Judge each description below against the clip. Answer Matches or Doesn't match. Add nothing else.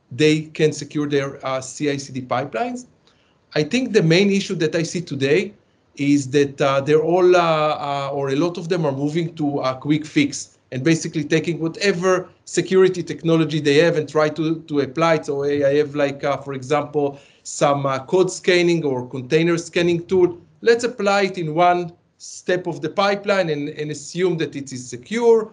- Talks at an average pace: Matches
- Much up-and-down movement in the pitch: Doesn't match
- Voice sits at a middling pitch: Matches